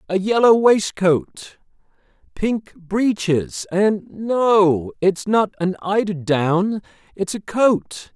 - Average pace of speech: No, slow, 105 wpm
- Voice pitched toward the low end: No, high, 195 Hz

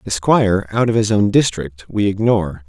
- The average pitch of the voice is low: Yes, low, 100 Hz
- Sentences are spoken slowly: No, average, 200 wpm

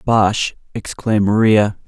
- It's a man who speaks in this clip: Yes, male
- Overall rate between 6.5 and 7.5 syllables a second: No, 3.9 syllables/s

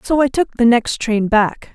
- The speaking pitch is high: Yes, high, 240 Hz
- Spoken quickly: Yes, fast, 240 wpm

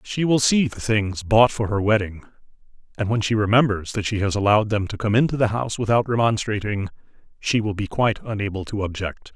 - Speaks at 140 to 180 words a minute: No, fast, 205 wpm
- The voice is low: Yes, low, 105 Hz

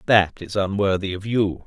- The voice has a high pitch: No, low, 100 Hz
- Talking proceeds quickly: No, average, 180 wpm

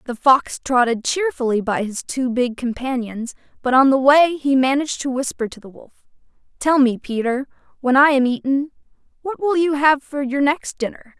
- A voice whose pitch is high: Yes, very high, 265 Hz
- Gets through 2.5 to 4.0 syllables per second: No, 5.2 syllables/s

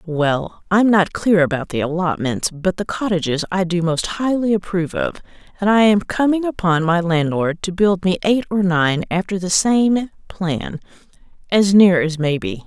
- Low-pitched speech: No, medium, 180 Hz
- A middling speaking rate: Yes, average, 180 wpm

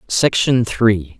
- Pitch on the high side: No, low, 110 Hz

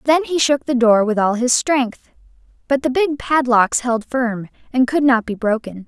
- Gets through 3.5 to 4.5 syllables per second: Yes, 4.4 syllables/s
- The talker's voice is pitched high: Yes, very high, 250 Hz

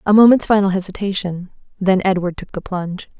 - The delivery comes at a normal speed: Yes, average, 170 wpm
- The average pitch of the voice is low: No, high, 190 Hz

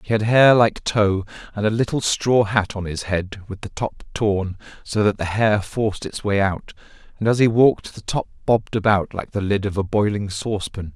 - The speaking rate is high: Yes, fast, 220 wpm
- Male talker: Yes, male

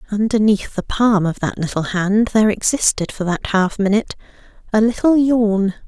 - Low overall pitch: No, high, 210 Hz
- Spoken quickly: No, average, 165 wpm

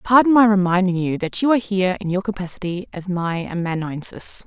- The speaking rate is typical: Yes, average, 190 wpm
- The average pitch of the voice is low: No, high, 190 Hz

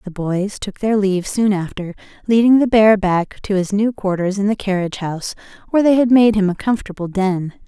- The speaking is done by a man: No, female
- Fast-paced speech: Yes, fast, 210 wpm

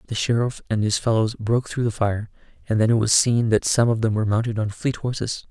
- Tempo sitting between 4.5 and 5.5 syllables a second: No, 6.0 syllables/s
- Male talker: Yes, male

